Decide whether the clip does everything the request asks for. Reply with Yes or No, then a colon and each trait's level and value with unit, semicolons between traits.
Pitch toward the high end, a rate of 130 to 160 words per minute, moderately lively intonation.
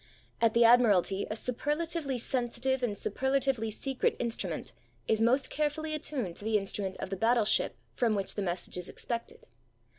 Yes: high, 235 Hz; average, 155 wpm; average, 4.3 semitones